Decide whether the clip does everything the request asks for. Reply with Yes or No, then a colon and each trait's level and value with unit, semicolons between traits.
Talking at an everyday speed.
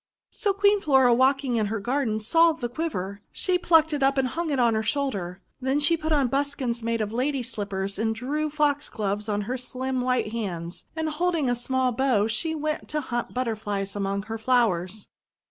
Yes: average, 190 wpm